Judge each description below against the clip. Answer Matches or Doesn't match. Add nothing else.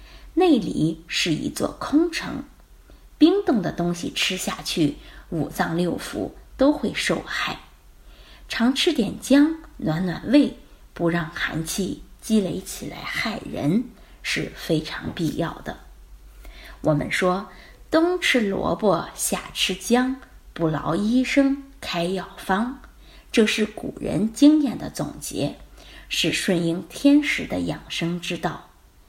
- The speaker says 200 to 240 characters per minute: Doesn't match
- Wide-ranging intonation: Matches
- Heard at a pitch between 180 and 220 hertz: Matches